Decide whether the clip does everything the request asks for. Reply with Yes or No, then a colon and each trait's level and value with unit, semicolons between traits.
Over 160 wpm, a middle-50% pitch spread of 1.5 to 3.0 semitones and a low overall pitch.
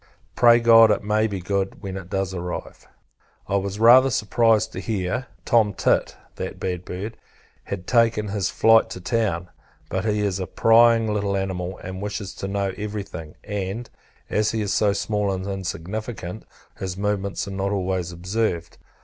Yes: average, 170 wpm; narrow, 2.6 semitones; low, 100 Hz